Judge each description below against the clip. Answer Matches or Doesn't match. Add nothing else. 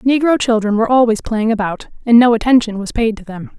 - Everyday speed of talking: Doesn't match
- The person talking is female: Matches